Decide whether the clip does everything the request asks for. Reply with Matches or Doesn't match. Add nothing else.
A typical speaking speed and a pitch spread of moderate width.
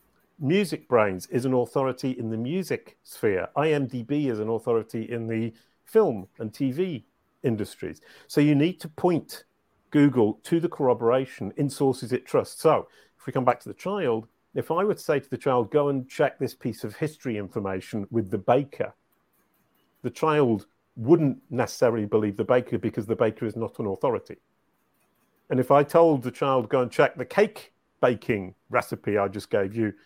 Matches